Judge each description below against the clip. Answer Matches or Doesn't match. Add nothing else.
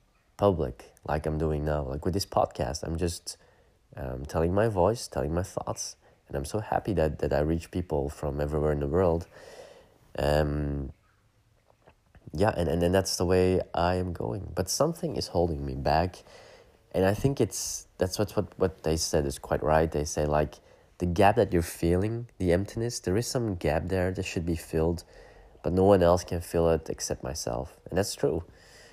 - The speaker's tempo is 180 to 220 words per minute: Matches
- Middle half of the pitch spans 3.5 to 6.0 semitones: Matches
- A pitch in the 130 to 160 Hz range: Doesn't match